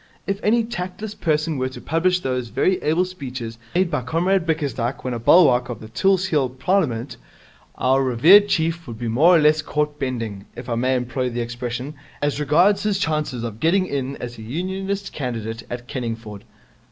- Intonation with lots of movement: Yes, wide, 6.4 semitones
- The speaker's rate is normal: Yes, average, 180 wpm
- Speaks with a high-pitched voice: No, medium, 140 Hz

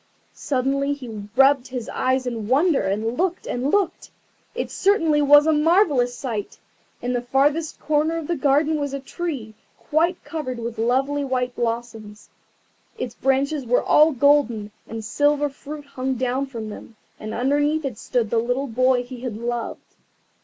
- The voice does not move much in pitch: No, average, 3.5 semitones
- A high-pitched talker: Yes, very high, 265 Hz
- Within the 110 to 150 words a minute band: No, average, 160 wpm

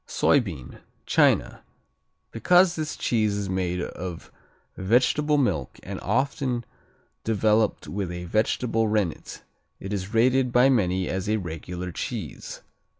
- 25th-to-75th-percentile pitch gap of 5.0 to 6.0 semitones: Yes, average, 5.3 semitones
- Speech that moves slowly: Yes, slow, 120 wpm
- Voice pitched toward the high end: No, low, 105 Hz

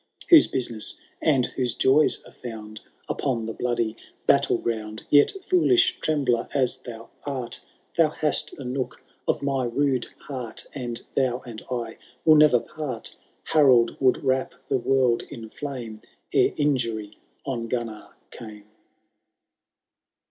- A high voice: No, low, 125 Hz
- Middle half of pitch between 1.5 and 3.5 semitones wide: Yes, average, 3.2 semitones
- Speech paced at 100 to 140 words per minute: Yes, slow, 135 wpm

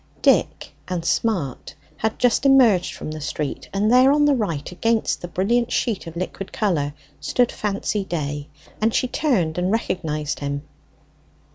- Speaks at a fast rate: No, average, 155 wpm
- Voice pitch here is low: No, high, 190 Hz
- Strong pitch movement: Yes, wide, 6.5 semitones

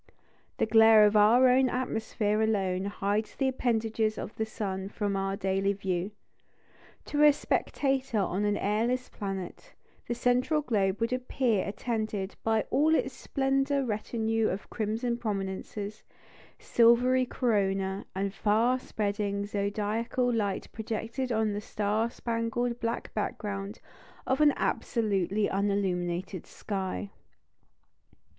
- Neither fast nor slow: No, slow, 120 wpm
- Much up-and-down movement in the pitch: No, average, 3.2 semitones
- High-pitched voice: Yes, high, 215 Hz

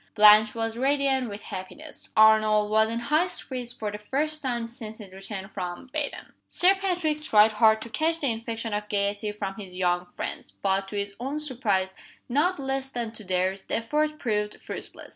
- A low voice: No, high, 220 Hz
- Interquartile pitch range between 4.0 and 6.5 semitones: Yes, average, 4.5 semitones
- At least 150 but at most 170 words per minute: No, average, 185 wpm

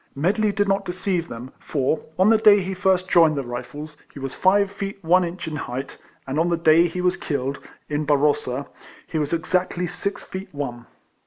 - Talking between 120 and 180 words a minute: No, average, 195 wpm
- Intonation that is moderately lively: Yes, average, 4.6 semitones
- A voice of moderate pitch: Yes, medium, 170 Hz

